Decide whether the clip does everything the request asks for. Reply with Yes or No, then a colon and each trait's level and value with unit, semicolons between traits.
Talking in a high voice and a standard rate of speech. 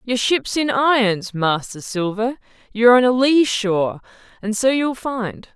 Yes: high, 230 Hz; average, 160 wpm